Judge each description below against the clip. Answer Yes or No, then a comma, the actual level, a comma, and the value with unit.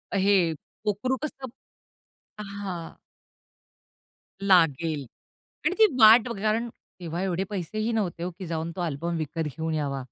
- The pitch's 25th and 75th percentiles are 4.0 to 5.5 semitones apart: Yes, average, 4.5 semitones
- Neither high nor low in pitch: Yes, medium, 180 Hz